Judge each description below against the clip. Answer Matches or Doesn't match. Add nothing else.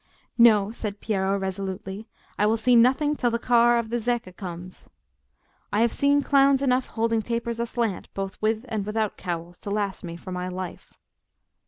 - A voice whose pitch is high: Matches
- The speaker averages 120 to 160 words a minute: Doesn't match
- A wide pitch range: Doesn't match